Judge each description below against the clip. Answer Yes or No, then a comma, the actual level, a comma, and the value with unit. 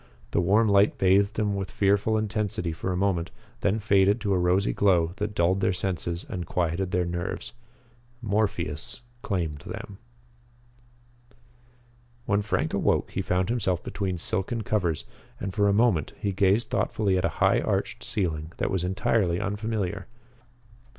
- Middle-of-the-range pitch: No, very low, 95 Hz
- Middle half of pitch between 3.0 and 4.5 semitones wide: No, narrow, 2.4 semitones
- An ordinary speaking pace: Yes, average, 150 wpm